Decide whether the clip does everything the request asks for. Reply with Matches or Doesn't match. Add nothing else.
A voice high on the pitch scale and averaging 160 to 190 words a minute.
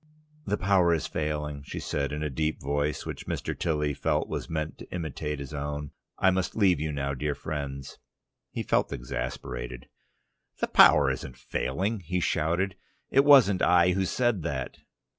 Doesn't match